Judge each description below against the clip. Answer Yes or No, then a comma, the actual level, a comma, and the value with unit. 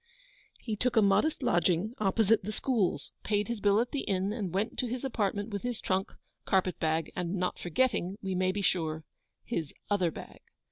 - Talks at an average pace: Yes, average, 190 wpm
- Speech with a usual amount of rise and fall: Yes, average, 3.6 semitones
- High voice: Yes, high, 200 Hz